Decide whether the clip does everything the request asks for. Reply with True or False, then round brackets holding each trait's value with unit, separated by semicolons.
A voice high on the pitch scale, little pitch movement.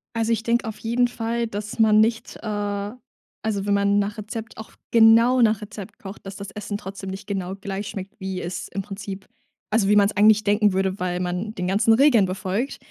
True (205 Hz; 2.3 semitones)